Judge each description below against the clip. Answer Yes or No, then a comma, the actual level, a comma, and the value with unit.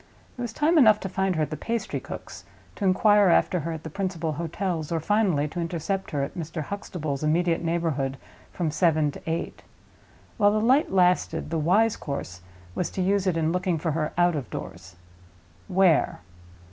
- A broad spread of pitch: No, average, 3.7 semitones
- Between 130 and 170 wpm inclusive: No, average, 185 wpm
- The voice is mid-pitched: Yes, medium, 170 Hz